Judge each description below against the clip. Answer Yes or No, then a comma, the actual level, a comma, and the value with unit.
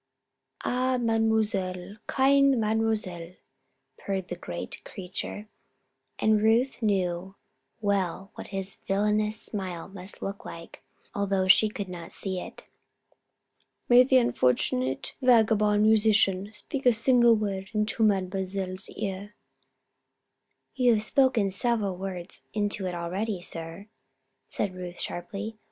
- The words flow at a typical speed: No, slow, 115 wpm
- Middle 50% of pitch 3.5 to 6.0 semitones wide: No, average, 3.0 semitones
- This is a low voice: No, high, 205 Hz